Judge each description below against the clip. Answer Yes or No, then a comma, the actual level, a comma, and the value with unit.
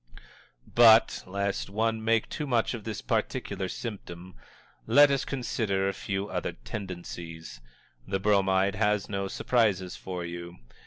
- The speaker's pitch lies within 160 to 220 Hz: No, low, 100 Hz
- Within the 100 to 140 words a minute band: Yes, slow, 135 wpm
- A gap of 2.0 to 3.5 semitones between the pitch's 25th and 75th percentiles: Yes, average, 3.2 semitones